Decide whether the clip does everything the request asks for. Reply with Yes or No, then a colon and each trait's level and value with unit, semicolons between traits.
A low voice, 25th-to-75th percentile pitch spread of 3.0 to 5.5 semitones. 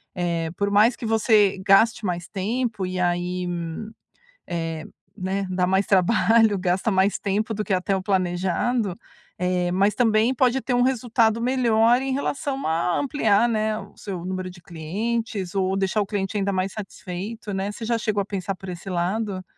No: high, 200 Hz; average, 3.4 semitones